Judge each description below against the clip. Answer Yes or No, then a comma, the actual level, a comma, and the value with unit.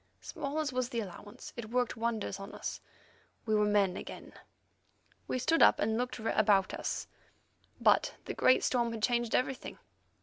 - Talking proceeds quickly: No, average, 165 wpm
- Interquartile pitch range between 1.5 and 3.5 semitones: Yes, average, 3.0 semitones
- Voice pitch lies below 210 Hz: No, high, 230 Hz